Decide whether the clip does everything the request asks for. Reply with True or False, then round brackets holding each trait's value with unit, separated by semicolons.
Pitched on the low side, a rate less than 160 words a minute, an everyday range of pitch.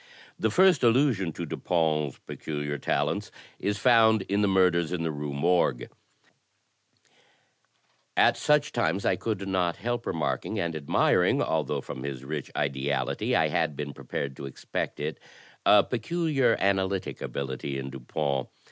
False (85 Hz; 145 wpm; 6.4 semitones)